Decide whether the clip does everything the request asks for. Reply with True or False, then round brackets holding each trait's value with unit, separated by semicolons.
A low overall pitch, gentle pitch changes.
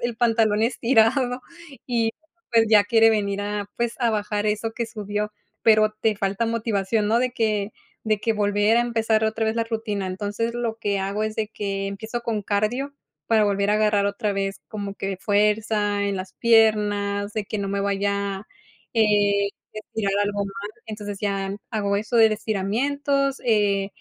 False (210 Hz; 1.9 semitones)